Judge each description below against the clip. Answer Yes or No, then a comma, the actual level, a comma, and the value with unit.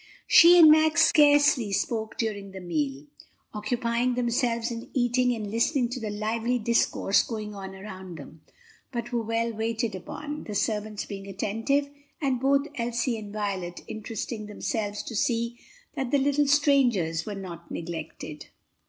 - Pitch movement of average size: Yes, average, 3.6 semitones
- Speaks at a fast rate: No, average, 150 wpm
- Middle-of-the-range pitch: No, high, 230 Hz